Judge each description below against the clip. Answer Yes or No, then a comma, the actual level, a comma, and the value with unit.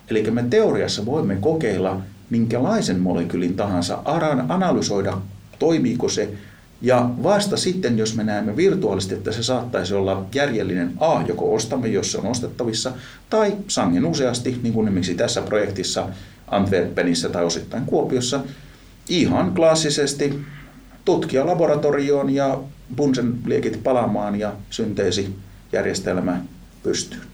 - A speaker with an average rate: Yes, average, 115 wpm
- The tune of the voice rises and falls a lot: Yes, wide, 6.2 semitones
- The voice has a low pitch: Yes, low, 115 Hz